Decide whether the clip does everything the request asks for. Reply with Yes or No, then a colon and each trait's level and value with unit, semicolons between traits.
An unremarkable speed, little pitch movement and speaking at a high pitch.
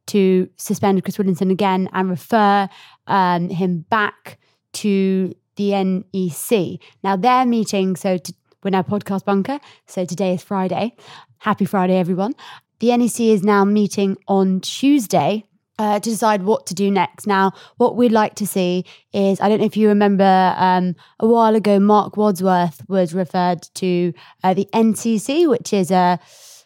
Yes: average, 160 wpm; narrow, 2.2 semitones; high, 195 Hz